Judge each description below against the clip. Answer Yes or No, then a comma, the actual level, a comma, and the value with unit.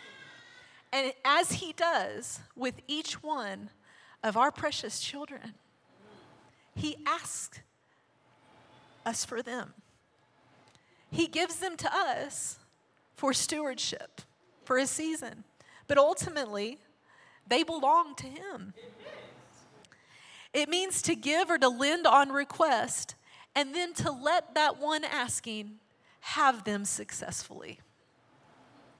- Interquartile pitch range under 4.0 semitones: No, average, 4.3 semitones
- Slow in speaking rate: Yes, slow, 105 wpm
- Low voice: No, very high, 290 Hz